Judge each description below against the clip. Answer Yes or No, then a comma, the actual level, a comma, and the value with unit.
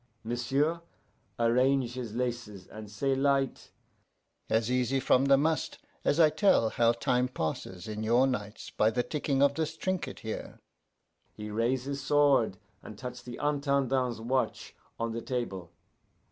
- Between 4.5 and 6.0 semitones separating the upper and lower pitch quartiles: No, average, 3.4 semitones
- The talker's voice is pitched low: Yes, low, 125 Hz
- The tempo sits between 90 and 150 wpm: Yes, average, 145 wpm